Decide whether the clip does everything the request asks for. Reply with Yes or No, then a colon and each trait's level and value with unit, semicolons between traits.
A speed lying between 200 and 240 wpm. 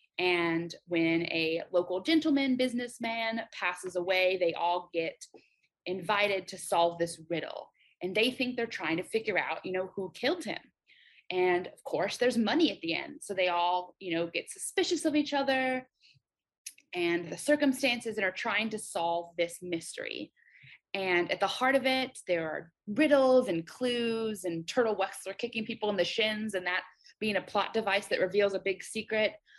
No: average, 175 wpm